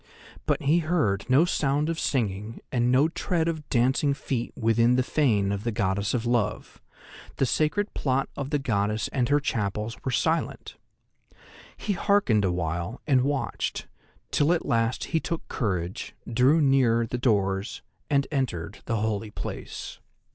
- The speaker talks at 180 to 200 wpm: No, average, 155 wpm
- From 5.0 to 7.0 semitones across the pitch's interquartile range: Yes, average, 5.3 semitones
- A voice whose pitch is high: No, low, 125 Hz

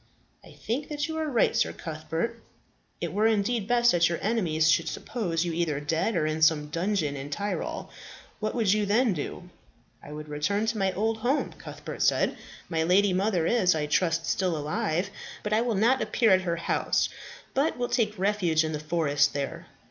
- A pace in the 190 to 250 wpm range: Yes, average, 195 wpm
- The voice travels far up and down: Yes, wide, 5.7 semitones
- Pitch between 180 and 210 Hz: Yes, medium, 185 Hz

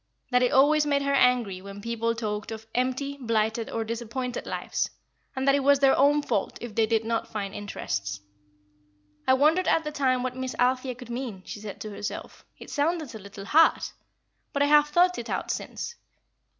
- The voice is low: No, very high, 250 Hz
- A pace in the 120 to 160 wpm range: No, average, 195 wpm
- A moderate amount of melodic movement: Yes, average, 4.2 semitones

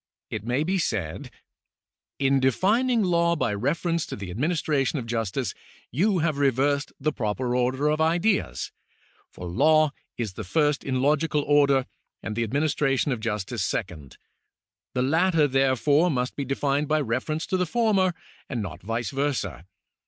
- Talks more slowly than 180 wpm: Yes, average, 160 wpm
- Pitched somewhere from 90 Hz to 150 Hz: Yes, medium, 140 Hz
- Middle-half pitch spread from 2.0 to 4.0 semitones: No, average, 4.7 semitones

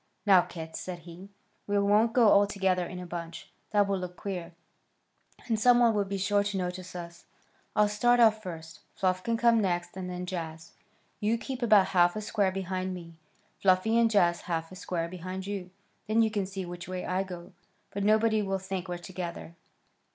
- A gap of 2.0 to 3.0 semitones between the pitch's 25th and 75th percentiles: Yes, average, 2.7 semitones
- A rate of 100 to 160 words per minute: No, average, 200 wpm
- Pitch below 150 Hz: No, high, 190 Hz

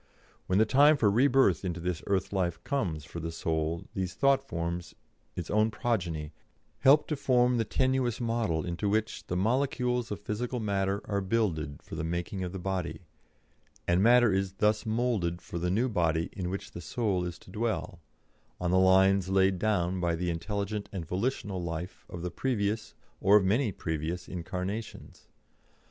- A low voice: Yes, very low, 95 Hz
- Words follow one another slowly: No, average, 175 wpm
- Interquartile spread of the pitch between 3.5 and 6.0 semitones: Yes, average, 4.4 semitones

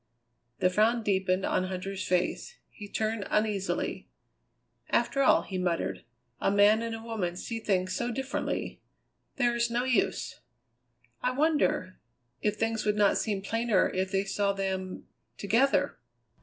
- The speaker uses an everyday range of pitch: Yes, average, 3.4 semitones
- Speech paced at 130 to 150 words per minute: Yes, average, 140 wpm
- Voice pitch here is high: Yes, high, 205 Hz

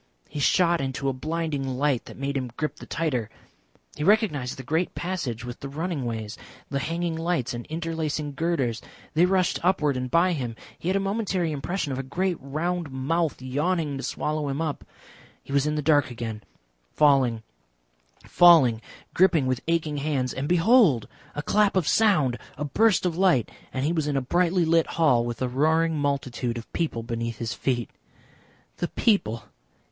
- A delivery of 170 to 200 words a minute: Yes, average, 180 wpm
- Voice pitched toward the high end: No, medium, 150 Hz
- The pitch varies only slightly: No, average, 4.7 semitones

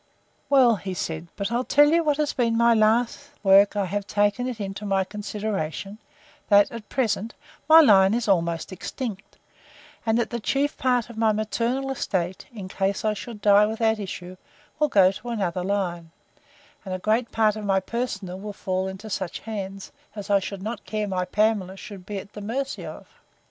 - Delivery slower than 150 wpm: No, average, 185 wpm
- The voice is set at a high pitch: Yes, high, 210 Hz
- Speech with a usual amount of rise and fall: Yes, average, 3.2 semitones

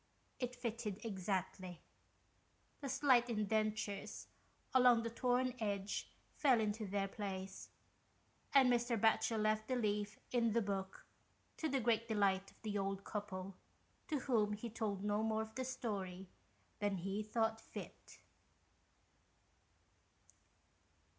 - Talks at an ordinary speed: No, slow, 125 wpm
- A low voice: No, high, 215 Hz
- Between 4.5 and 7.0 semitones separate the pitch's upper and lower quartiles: No, average, 3.0 semitones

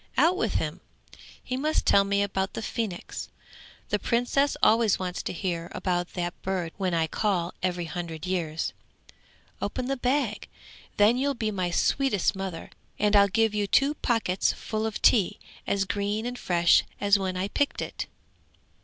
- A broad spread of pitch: No, average, 4.1 semitones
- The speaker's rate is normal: Yes, average, 165 wpm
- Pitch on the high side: Yes, high, 200 Hz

